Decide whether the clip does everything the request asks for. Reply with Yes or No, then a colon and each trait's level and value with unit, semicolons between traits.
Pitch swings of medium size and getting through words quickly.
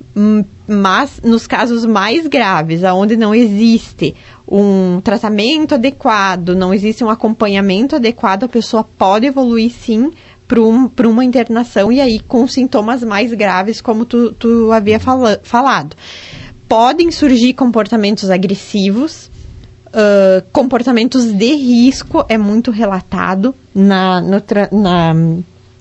No: average, 3.6 semitones; slow, 120 wpm